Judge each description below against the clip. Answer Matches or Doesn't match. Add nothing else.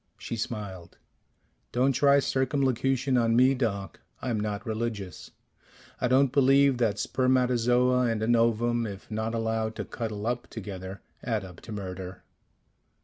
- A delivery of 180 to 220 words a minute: Doesn't match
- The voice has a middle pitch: Doesn't match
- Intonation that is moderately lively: Matches